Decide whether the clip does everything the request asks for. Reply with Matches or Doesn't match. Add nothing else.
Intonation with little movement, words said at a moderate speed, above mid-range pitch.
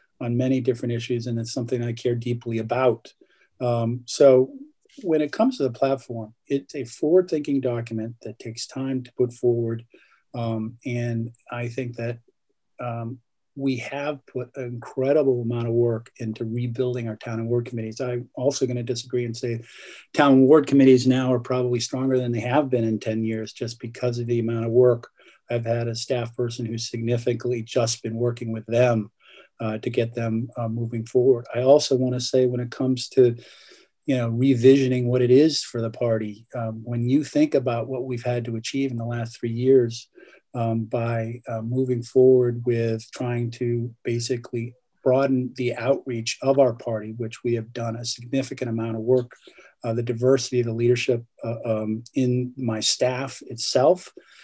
Doesn't match